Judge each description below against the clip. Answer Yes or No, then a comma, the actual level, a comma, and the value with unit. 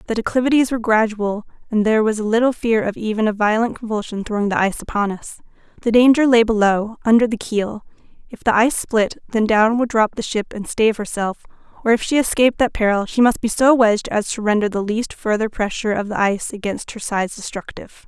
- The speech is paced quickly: Yes, fast, 210 wpm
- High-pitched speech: Yes, high, 220 Hz